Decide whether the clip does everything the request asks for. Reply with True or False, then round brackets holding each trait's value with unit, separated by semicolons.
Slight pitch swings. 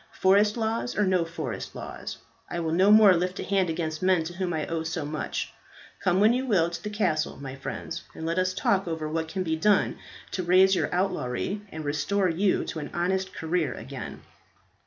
False (3.2 semitones)